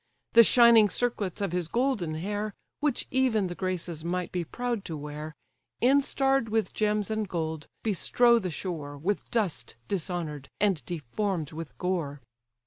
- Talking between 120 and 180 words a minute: Yes, average, 145 wpm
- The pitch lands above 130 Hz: Yes, high, 190 Hz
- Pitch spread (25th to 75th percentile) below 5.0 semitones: No, wide, 5.5 semitones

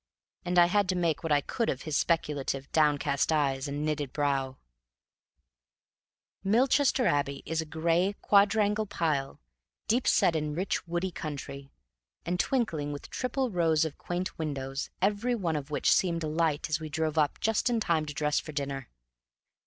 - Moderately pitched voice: Yes, medium, 160 Hz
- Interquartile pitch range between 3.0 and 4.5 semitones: Yes, average, 4.2 semitones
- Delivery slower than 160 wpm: No, average, 165 wpm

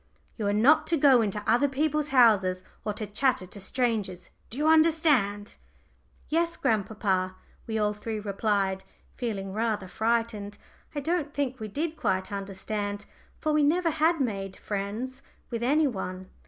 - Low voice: No, high, 220 Hz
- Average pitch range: No, wide, 6.0 semitones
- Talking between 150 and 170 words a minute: Yes, average, 155 wpm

